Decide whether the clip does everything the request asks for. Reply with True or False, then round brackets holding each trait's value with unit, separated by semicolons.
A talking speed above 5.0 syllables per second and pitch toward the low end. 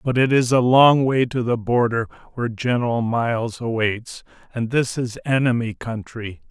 False (4.7 syllables/s; 120 Hz)